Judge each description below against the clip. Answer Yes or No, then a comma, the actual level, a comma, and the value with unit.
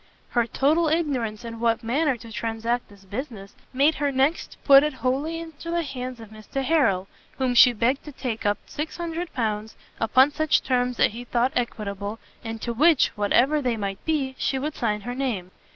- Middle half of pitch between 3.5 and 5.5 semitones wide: Yes, average, 4.3 semitones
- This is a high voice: Yes, very high, 250 Hz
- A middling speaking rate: Yes, average, 190 wpm